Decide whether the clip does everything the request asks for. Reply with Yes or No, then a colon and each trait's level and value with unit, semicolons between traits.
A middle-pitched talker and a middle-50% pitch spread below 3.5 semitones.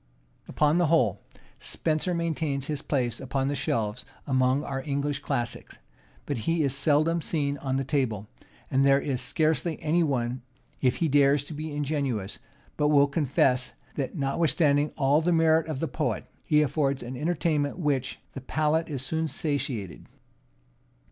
Yes: medium, 145 Hz; average, 2.8 semitones